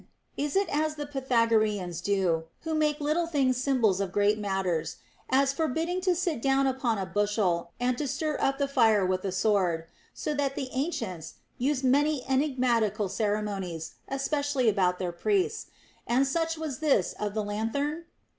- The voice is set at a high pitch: Yes, very high, 255 Hz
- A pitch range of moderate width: No, wide, 6.2 semitones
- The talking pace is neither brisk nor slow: Yes, average, 175 wpm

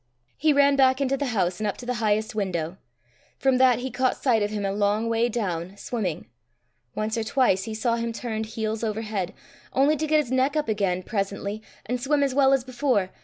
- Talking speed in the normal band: No, fast, 220 wpm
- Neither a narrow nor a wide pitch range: Yes, average, 4.1 semitones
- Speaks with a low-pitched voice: No, high, 225 Hz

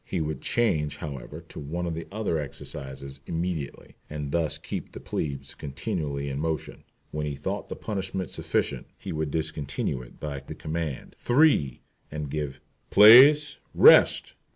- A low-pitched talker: Yes, very low, 75 Hz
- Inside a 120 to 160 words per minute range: Yes, average, 150 wpm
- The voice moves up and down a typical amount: Yes, average, 3.7 semitones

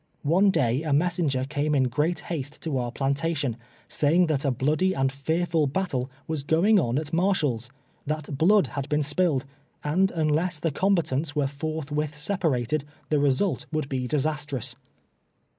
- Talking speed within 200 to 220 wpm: No, average, 165 wpm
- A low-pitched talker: No, medium, 150 Hz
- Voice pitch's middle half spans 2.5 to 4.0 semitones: Yes, average, 3.3 semitones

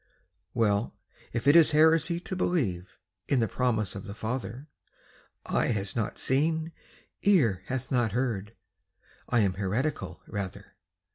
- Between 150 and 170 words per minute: No, slow, 135 wpm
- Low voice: Yes, low, 120 Hz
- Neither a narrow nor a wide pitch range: No, wide, 6.2 semitones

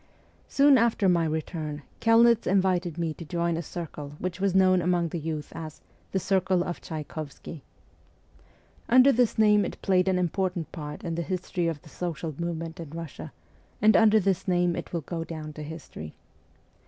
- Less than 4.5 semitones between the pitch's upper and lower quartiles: Yes, average, 3.0 semitones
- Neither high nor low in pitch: Yes, medium, 175 Hz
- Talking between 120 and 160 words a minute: No, average, 180 wpm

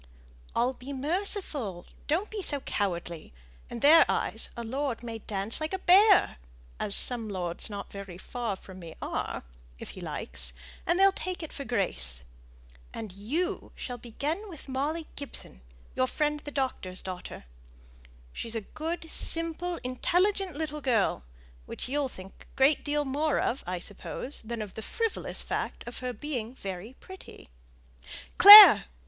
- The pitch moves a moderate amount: No, wide, 7.7 semitones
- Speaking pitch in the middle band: No, very high, 260 Hz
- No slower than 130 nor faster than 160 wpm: Yes, average, 155 wpm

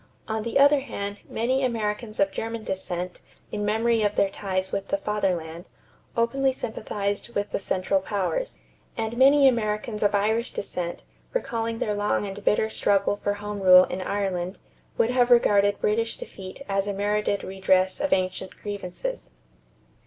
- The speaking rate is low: No, average, 155 wpm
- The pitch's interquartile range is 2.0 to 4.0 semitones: Yes, average, 2.9 semitones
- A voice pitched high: Yes, high, 205 Hz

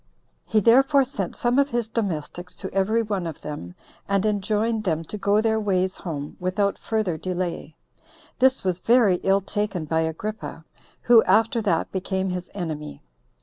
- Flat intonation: No, average, 3.8 semitones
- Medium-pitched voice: No, high, 195 Hz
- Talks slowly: No, average, 160 wpm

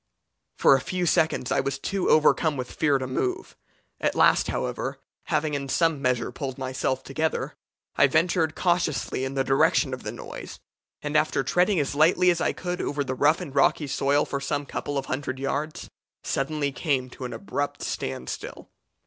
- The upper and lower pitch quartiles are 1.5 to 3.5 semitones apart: Yes, average, 2.9 semitones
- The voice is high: No, medium, 145 Hz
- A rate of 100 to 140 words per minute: No, average, 180 wpm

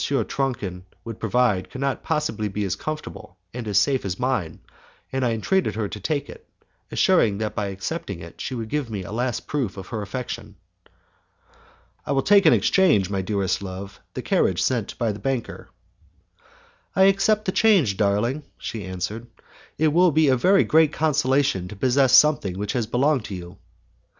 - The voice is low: Yes, low, 115 Hz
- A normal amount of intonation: No, wide, 6.1 semitones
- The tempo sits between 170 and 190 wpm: Yes, average, 180 wpm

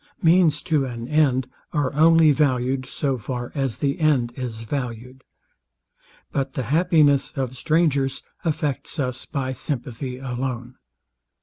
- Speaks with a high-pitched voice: No, low, 135 Hz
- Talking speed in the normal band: No, slow, 125 wpm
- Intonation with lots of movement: No, average, 3.0 semitones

